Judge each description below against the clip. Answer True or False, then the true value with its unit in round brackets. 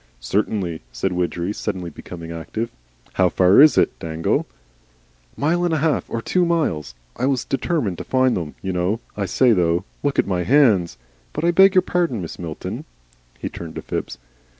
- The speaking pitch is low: True (100 Hz)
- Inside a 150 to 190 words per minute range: True (180 wpm)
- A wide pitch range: True (8.7 semitones)